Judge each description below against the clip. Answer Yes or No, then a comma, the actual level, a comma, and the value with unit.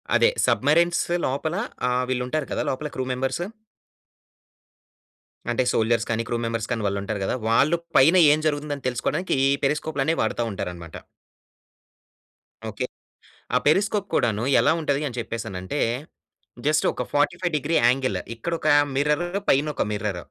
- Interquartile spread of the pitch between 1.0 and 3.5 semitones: No, average, 4.9 semitones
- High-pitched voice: No, low, 135 Hz